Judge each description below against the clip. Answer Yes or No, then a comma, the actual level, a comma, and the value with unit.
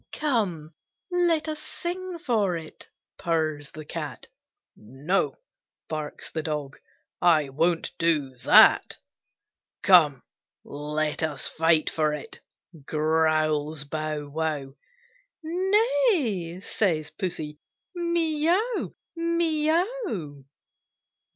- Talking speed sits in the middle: No, slow, 95 wpm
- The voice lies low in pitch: No, medium, 165 Hz